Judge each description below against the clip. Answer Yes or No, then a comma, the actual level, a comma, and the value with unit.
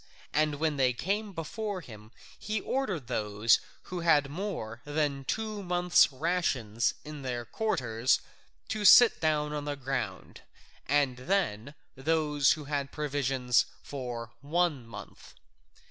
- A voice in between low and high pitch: Yes, medium, 145 Hz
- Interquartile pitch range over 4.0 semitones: Yes, wide, 5.6 semitones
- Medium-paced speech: No, slow, 130 wpm